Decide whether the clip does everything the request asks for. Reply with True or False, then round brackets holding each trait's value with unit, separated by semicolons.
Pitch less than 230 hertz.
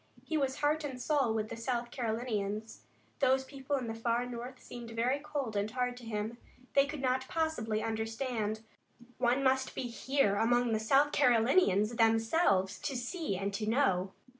False (240 Hz)